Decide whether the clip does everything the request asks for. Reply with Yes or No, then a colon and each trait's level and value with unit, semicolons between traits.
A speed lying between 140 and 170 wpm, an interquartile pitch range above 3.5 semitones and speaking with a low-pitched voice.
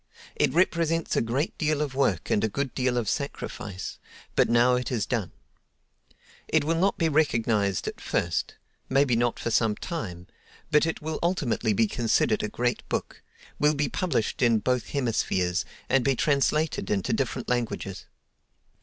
Yes: average, 155 wpm; wide, 5.4 semitones; low, 125 Hz